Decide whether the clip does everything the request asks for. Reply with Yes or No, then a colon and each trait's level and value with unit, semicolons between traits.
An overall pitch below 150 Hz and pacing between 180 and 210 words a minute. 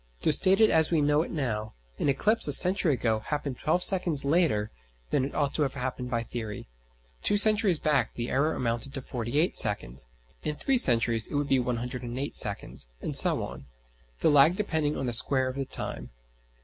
Yes: medium, 140 Hz; average, 200 wpm